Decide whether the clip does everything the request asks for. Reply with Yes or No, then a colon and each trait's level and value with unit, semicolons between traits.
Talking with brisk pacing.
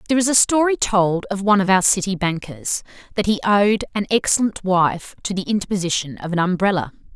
No: average, 195 wpm